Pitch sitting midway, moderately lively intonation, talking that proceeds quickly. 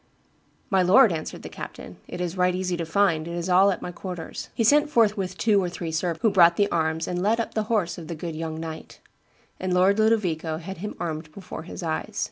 Yes: medium, 180 Hz; average, 3.4 semitones; fast, 230 wpm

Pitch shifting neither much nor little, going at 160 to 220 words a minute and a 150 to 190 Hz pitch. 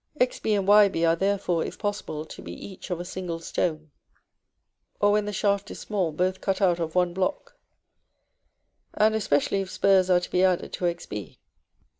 Yes: average, 3.0 semitones; average, 180 wpm; medium, 185 Hz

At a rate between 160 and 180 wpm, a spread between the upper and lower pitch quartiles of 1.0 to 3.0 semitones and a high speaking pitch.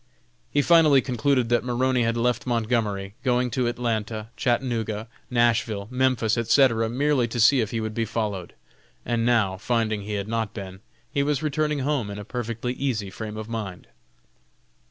No: average, 165 wpm; average, 2.7 semitones; low, 115 Hz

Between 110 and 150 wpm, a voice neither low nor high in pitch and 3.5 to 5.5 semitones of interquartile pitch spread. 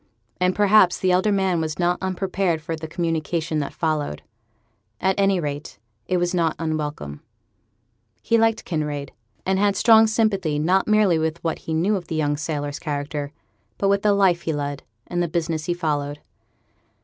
No: average, 175 wpm; medium, 170 Hz; average, 3.8 semitones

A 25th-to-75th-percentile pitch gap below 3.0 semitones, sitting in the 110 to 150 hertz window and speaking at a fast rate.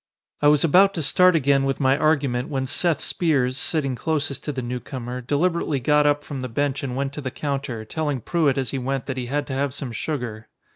Yes: narrow, 2.5 semitones; medium, 140 Hz; fast, 225 wpm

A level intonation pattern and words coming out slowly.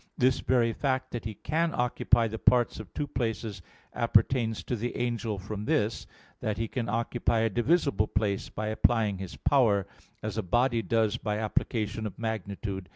No: narrow, 2.3 semitones; average, 170 wpm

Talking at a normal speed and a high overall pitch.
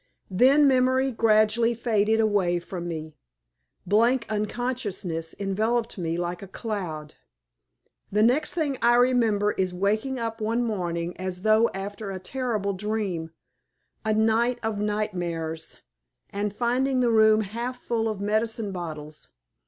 No: slow, 130 wpm; high, 215 Hz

